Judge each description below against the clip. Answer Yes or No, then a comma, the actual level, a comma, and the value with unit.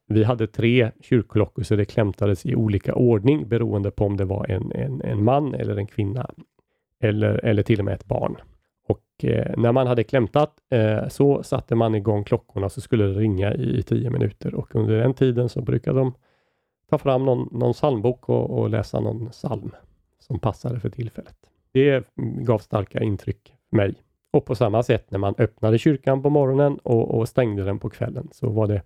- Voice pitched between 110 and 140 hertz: Yes, low, 115 Hz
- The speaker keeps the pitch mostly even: No, average, 3.5 semitones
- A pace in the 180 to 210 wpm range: Yes, fast, 195 wpm